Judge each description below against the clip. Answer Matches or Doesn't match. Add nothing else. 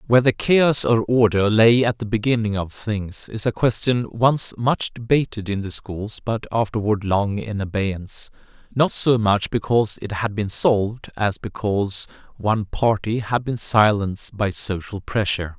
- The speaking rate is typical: Matches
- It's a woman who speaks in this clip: Doesn't match